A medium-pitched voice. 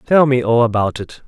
No: low, 120 Hz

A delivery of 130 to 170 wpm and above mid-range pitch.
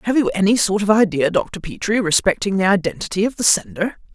No: fast, 205 wpm; high, 200 Hz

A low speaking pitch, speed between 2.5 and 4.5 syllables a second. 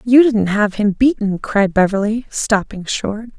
No: high, 215 Hz; 4.1 syllables/s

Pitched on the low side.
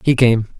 Yes: low, 120 Hz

